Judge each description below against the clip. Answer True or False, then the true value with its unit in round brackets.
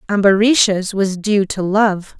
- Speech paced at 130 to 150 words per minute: True (135 wpm)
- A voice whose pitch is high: True (200 Hz)